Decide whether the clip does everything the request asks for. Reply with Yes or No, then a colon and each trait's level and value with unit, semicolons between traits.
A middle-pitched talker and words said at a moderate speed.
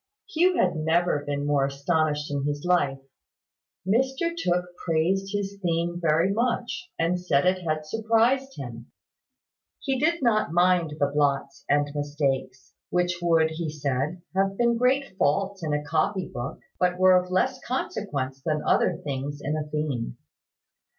Yes: medium, 170 Hz; average, 150 wpm